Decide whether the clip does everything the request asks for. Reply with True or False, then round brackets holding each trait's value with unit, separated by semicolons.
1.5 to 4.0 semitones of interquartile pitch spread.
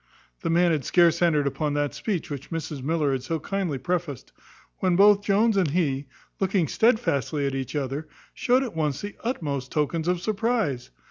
False (5.4 semitones)